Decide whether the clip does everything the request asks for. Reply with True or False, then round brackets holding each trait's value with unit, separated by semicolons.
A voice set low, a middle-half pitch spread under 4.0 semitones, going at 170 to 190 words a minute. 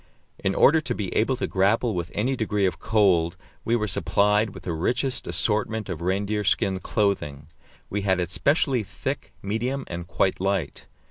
True (105 Hz; 3.2 semitones; 175 wpm)